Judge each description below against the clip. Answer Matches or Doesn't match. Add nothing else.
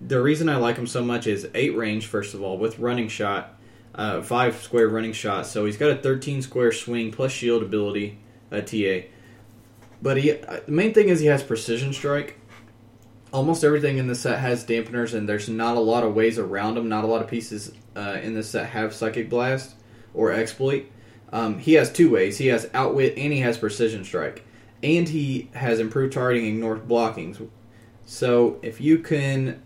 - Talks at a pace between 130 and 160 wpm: Doesn't match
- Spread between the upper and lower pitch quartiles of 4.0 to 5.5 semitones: Doesn't match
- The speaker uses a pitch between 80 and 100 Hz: Doesn't match